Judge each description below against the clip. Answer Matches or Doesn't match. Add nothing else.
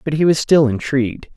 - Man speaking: Matches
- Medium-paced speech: Doesn't match